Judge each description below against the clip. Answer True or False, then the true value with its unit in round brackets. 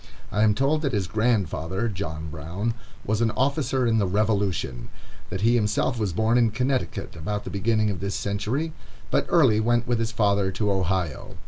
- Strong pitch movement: False (3.5 semitones)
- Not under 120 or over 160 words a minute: False (185 wpm)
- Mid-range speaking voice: False (105 Hz)